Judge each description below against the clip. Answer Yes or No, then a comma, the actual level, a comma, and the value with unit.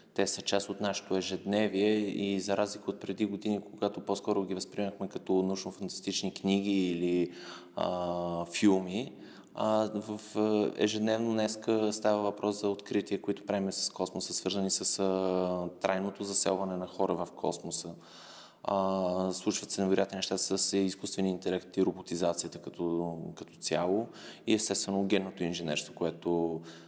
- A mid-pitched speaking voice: No, very low, 95 Hz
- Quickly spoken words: No, average, 135 wpm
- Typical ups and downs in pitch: No, narrow, 1.8 semitones